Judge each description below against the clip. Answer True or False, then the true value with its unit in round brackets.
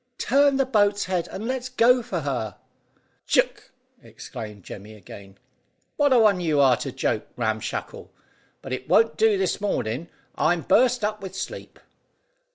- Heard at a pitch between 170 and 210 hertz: True (190 Hz)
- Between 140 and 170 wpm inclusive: True (160 wpm)